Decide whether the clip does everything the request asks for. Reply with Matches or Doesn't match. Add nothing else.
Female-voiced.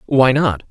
Doesn't match